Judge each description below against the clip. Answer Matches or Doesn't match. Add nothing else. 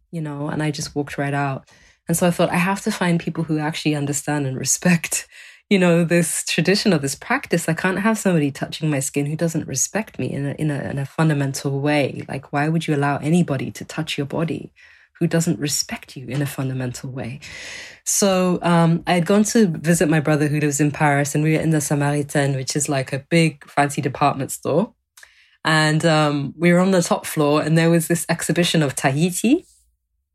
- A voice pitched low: Doesn't match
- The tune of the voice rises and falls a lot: Doesn't match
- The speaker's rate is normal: Doesn't match